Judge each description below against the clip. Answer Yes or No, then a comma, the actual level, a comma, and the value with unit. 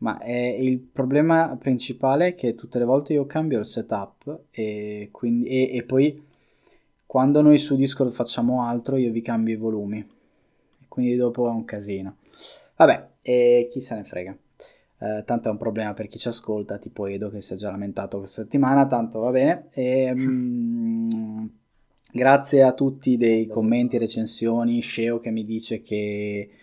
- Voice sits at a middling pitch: No, low, 120 Hz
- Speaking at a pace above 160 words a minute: Yes, fast, 170 wpm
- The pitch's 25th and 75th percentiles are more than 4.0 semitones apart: No, average, 3.0 semitones